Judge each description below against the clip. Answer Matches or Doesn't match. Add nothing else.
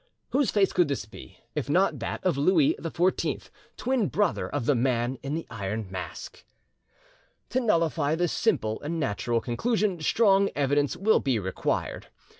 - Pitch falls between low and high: Matches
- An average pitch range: Doesn't match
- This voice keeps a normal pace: Matches